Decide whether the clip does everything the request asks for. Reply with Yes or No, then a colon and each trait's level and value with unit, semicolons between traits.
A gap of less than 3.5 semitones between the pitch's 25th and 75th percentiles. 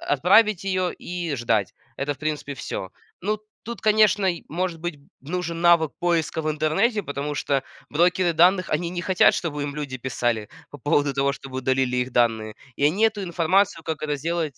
No: average, 4.4 semitones